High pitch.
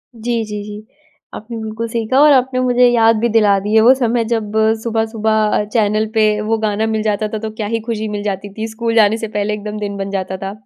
Yes: high, 220 Hz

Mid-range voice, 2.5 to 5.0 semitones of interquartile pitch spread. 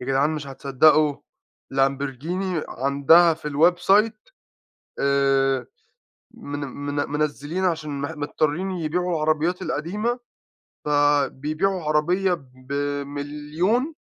Yes: medium, 150 Hz; average, 3.6 semitones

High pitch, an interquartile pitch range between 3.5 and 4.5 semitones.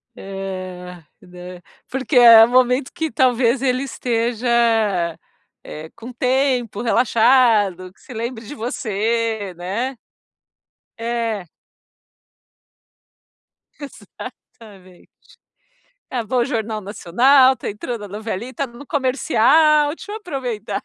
Yes: high, 235 Hz; average, 3.9 semitones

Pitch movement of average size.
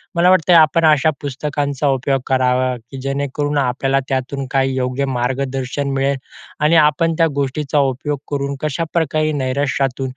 No: narrow, 2.2 semitones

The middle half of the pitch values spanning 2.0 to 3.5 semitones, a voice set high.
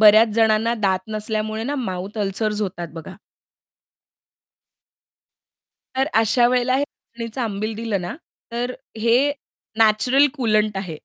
Yes: narrow, 2.4 semitones; high, 220 Hz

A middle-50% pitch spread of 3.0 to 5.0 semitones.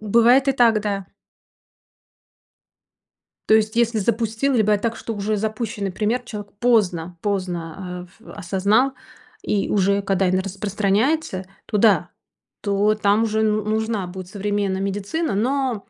No: narrow, 2.4 semitones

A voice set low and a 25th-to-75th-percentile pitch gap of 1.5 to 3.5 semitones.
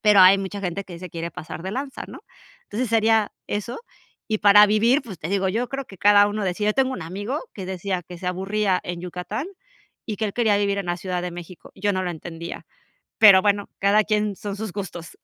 No: high, 200 Hz; average, 2.8 semitones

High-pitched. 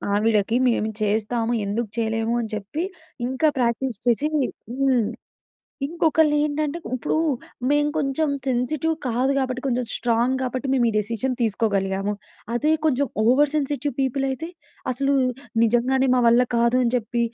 Yes: very high, 250 Hz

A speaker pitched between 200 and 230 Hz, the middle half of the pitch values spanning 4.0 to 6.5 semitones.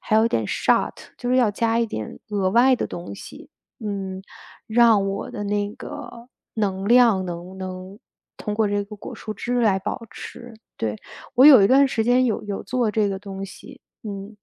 No: high, 210 Hz; average, 3.2 semitones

